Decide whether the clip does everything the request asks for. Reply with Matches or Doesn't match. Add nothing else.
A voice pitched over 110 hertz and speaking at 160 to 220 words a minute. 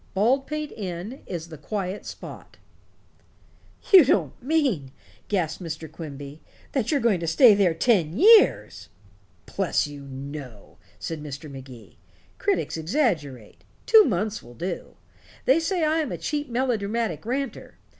Doesn't match